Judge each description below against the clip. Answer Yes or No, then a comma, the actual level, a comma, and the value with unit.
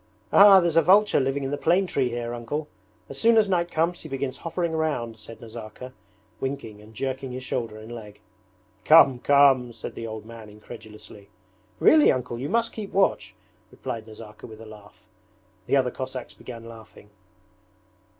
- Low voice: Yes, low, 130 Hz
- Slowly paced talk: No, average, 170 wpm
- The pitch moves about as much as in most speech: No, wide, 5.8 semitones